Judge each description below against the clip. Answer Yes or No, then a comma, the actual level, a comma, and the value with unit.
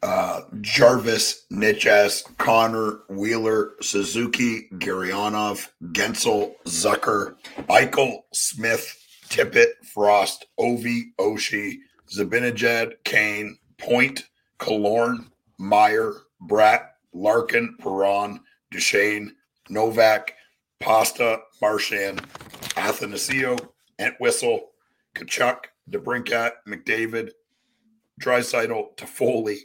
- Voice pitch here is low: Yes, low, 115 Hz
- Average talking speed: No, slow, 70 wpm